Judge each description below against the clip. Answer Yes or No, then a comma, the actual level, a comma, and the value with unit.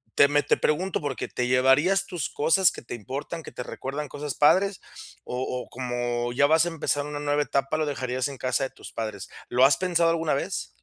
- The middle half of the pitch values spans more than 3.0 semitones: Yes, average, 4.1 semitones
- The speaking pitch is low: No, medium, 145 Hz